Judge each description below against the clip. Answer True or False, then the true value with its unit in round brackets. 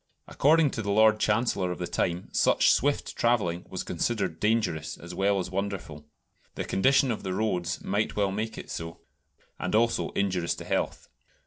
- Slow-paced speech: False (175 wpm)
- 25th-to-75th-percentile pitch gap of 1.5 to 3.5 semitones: False (4.0 semitones)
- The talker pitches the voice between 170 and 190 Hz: False (100 Hz)